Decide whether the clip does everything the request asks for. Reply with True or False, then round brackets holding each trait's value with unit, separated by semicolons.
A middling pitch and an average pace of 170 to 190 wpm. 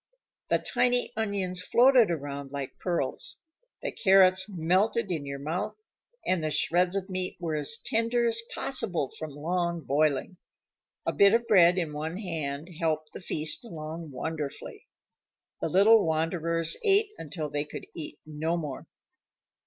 False (170 Hz; 145 wpm)